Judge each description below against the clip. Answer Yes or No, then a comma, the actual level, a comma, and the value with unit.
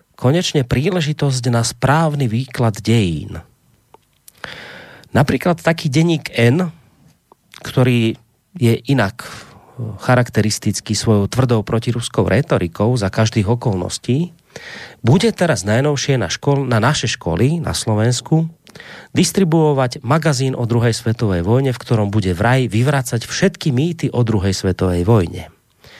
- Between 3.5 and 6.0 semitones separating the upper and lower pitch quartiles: Yes, average, 4.7 semitones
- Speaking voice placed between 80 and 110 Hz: No, low, 125 Hz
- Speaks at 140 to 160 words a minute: No, slow, 110 wpm